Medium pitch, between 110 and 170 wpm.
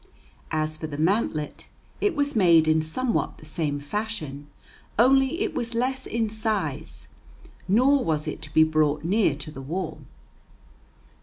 Yes: medium, 170 Hz; average, 150 wpm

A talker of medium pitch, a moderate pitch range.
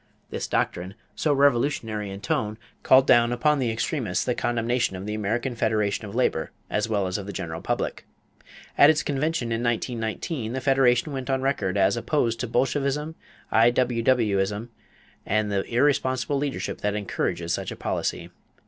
No: low, 120 Hz; average, 4.0 semitones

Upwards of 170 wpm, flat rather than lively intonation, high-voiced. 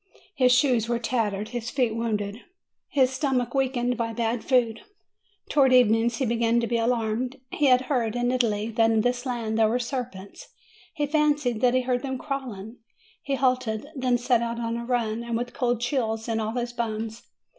Yes: average, 190 wpm; narrow, 2.1 semitones; high, 240 Hz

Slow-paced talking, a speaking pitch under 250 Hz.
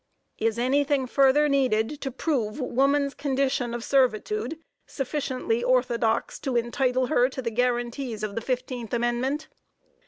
No: slow, 130 wpm; very high, 255 Hz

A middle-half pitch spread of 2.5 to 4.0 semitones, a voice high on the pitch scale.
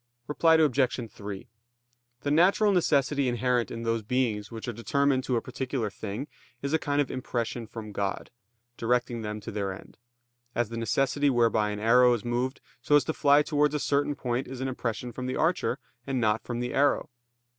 No: average, 3.6 semitones; low, 125 Hz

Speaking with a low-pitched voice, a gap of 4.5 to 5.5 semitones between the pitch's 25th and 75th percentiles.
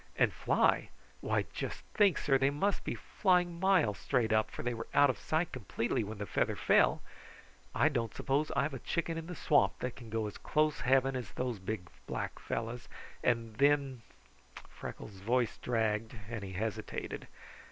Yes: low, 125 Hz; average, 4.8 semitones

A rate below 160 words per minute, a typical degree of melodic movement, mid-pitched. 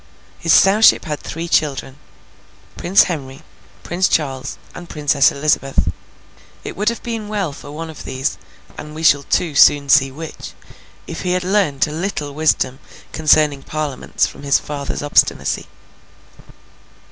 Yes: average, 145 wpm; average, 3.5 semitones; medium, 150 Hz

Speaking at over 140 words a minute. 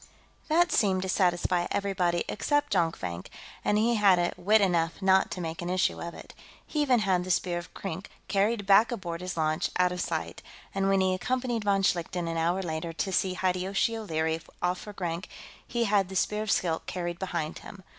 Yes: average, 195 wpm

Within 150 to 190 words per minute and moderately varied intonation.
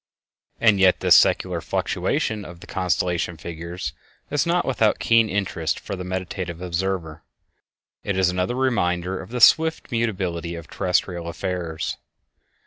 No: slow, 135 wpm; average, 3.4 semitones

